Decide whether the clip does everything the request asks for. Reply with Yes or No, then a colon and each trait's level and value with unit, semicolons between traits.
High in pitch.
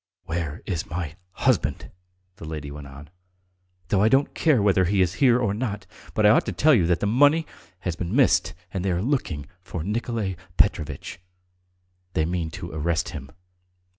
No: very low, 95 Hz